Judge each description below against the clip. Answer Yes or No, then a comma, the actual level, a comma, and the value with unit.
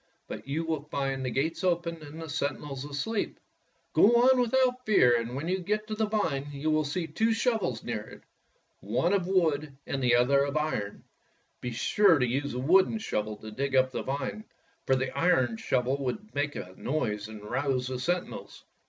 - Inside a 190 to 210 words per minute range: Yes, average, 195 wpm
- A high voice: No, medium, 145 Hz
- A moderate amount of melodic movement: No, wide, 5.9 semitones